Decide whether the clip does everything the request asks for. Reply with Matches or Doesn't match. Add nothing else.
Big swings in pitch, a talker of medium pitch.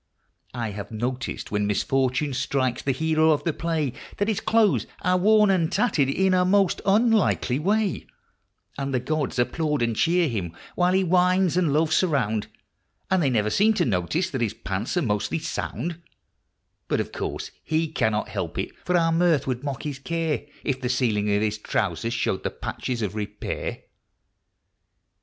Matches